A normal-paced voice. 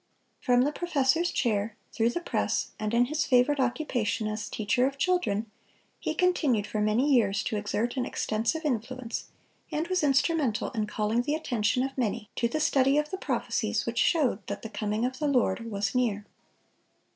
Yes: average, 180 wpm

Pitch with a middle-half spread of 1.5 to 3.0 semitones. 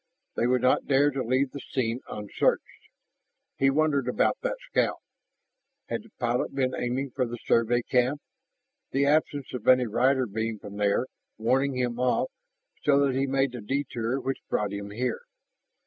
Yes: average, 2.7 semitones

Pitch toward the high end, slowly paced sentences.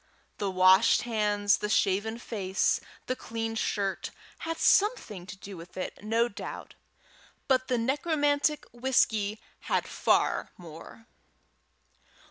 Yes: high, 220 Hz; slow, 115 wpm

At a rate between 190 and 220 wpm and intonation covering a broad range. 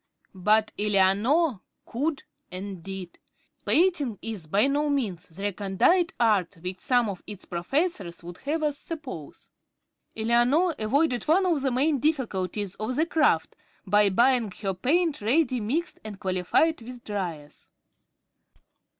No: slow, 135 wpm; wide, 7.2 semitones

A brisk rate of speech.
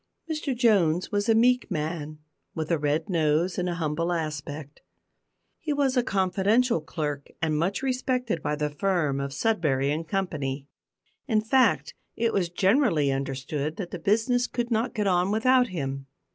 No: average, 160 wpm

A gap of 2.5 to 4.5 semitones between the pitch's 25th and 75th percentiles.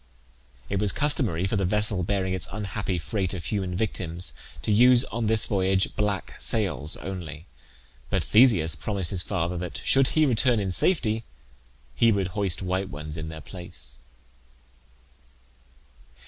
Yes: average, 3.6 semitones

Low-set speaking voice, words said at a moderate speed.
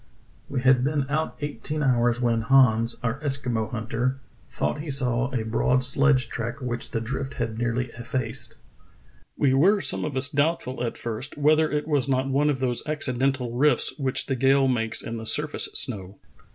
Yes: low, 130 Hz; average, 180 wpm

